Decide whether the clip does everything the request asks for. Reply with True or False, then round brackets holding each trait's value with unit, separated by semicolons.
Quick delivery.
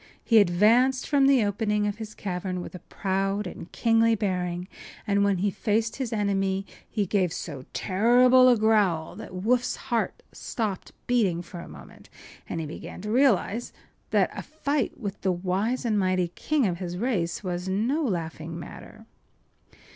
False (165 wpm)